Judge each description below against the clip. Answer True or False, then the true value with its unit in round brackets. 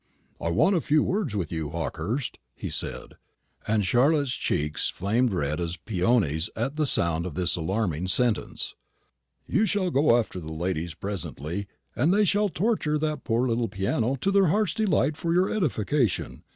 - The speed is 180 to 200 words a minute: False (165 wpm)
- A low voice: True (115 Hz)